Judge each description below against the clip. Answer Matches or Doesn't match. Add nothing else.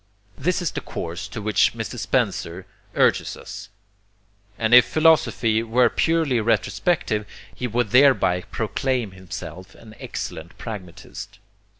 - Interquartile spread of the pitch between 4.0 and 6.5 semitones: Matches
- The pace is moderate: Doesn't match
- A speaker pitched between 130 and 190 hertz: Doesn't match